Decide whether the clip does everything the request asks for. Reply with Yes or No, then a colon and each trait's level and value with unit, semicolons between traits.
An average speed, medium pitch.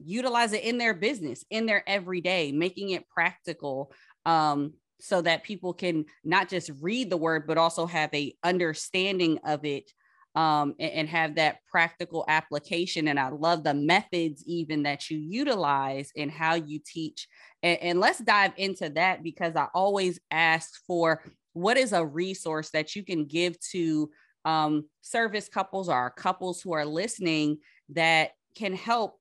Yes: average, 160 wpm; medium, 165 Hz